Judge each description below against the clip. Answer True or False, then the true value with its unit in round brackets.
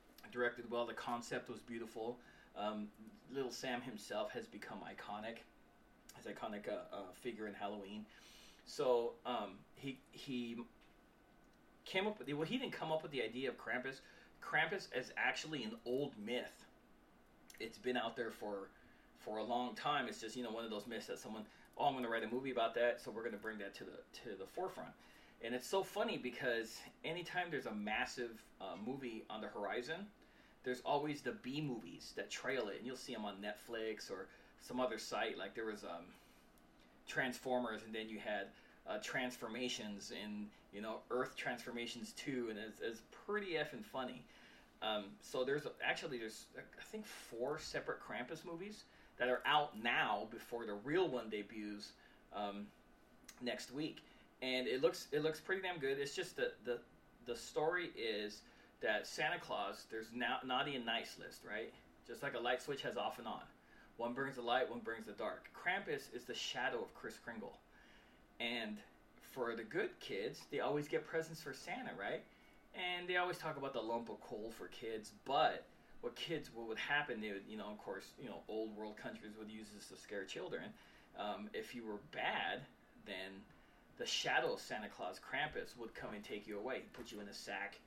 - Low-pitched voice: True (120 Hz)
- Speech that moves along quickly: False (195 wpm)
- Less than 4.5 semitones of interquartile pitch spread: False (5.0 semitones)